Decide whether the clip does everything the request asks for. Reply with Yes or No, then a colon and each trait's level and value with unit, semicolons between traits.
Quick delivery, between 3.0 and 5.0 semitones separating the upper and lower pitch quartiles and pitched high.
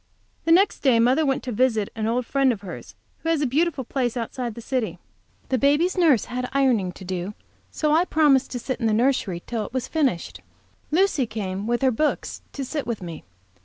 Yes: fast, 215 wpm; average, 4.3 semitones; very high, 255 Hz